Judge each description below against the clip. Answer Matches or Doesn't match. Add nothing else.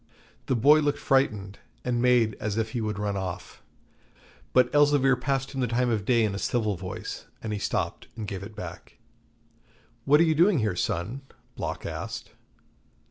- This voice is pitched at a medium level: Doesn't match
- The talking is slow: Doesn't match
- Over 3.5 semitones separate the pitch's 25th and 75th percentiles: Matches